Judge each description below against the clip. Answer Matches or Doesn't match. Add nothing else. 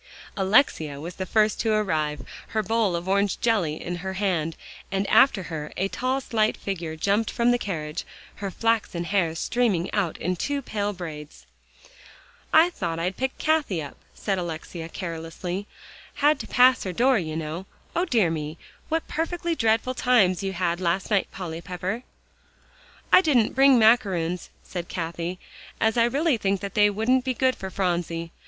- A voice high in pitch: Matches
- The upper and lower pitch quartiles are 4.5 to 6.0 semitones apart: Matches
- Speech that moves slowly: Doesn't match